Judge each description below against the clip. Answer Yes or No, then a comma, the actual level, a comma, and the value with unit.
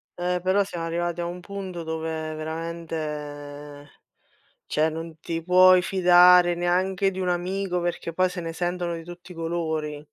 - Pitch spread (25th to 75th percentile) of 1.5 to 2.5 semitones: Yes, narrow, 2.0 semitones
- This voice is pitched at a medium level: Yes, medium, 175 Hz